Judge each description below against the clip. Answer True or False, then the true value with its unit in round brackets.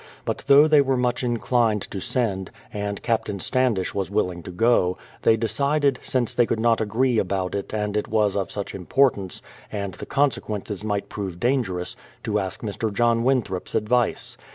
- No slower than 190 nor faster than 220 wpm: False (175 wpm)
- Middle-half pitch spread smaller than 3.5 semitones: False (3.8 semitones)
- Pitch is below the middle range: True (110 Hz)